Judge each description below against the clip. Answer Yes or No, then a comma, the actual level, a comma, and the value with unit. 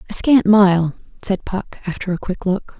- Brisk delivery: No, average, 195 wpm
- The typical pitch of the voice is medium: No, high, 195 Hz